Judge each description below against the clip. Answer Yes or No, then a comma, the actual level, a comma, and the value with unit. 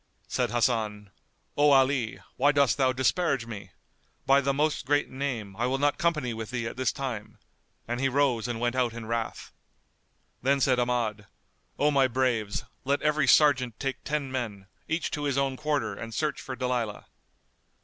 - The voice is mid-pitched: No, low, 130 Hz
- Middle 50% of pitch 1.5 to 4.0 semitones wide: Yes, average, 3.3 semitones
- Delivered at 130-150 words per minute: No, average, 175 wpm